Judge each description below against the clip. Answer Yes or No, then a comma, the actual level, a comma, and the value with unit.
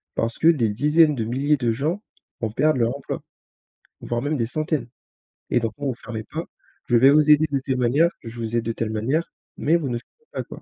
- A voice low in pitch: Yes, low, 130 Hz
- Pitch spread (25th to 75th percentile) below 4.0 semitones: No, average, 4.6 semitones